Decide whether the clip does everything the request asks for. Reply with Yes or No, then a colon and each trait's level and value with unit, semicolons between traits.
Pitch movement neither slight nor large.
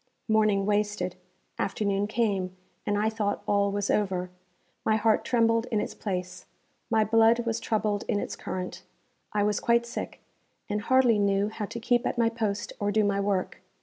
No: narrow, 2.0 semitones